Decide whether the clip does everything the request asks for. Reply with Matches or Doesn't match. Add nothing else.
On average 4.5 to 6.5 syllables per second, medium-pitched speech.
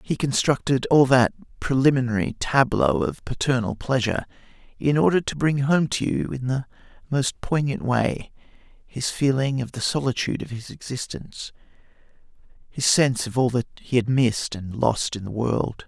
Doesn't match